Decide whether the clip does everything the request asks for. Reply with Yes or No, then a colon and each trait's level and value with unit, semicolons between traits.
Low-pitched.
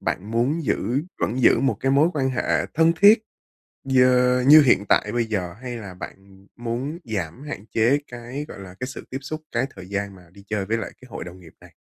Yes: low, 120 Hz